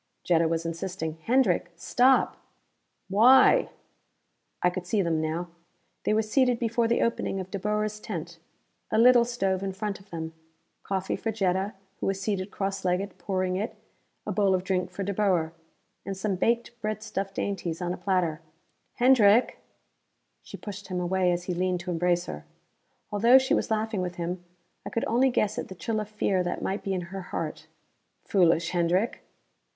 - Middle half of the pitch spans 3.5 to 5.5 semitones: No, average, 3.1 semitones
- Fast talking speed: No, average, 175 wpm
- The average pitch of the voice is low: No, high, 190 Hz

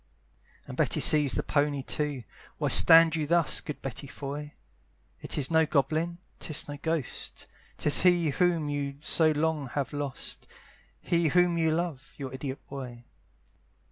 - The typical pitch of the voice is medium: Yes, medium, 150 Hz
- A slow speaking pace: No, average, 150 wpm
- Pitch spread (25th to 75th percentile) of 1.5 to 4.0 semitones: Yes, narrow, 2.6 semitones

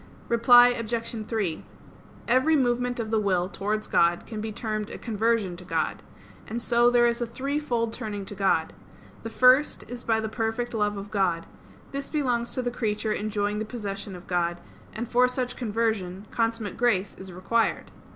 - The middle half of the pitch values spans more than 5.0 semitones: No, average, 2.9 semitones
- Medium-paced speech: Yes, average, 175 wpm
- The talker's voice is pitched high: Yes, high, 225 Hz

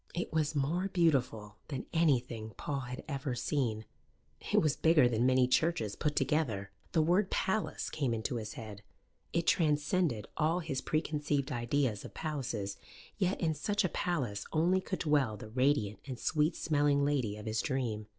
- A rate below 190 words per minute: Yes, average, 165 wpm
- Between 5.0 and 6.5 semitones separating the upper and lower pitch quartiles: Yes, average, 5.3 semitones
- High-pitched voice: No, medium, 140 Hz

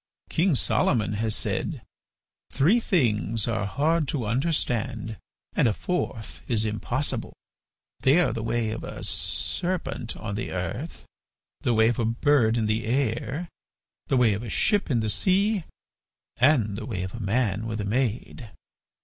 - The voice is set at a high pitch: No, low, 115 Hz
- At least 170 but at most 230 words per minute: No, average, 160 wpm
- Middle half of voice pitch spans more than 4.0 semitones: Yes, average, 4.7 semitones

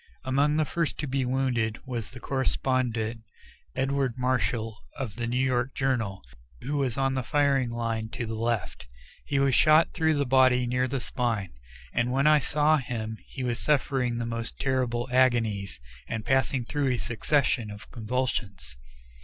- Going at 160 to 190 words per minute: Yes, average, 165 wpm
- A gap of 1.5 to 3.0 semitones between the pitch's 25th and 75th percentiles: Yes, average, 2.7 semitones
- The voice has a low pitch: Yes, low, 125 Hz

